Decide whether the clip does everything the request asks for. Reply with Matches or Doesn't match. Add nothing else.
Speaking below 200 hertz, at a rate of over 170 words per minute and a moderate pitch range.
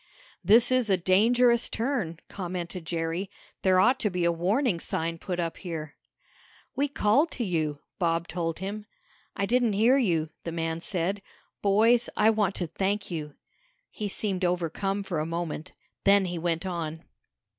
Doesn't match